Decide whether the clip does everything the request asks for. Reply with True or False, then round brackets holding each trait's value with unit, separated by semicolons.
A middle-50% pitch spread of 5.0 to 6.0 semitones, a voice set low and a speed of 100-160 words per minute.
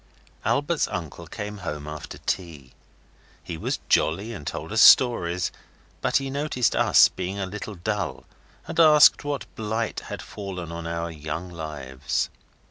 True (5.4 semitones; 90 Hz; 145 wpm)